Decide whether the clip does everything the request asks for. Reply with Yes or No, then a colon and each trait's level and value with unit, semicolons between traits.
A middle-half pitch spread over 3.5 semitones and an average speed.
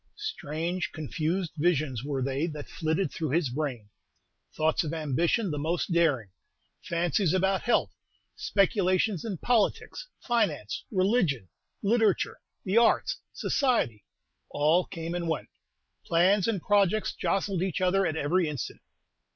No: average, 4.4 semitones; slow, 125 wpm